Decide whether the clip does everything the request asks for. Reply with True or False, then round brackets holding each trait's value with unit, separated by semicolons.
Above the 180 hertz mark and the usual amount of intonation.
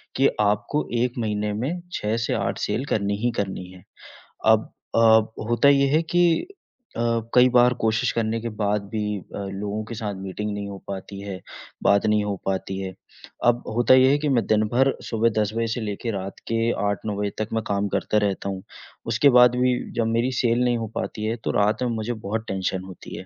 False (110 Hz; 3.1 semitones)